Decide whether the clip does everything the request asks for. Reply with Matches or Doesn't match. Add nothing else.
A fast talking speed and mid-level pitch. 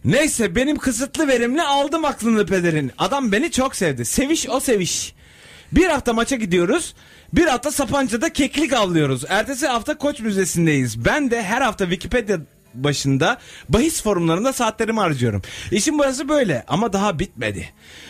Doesn't match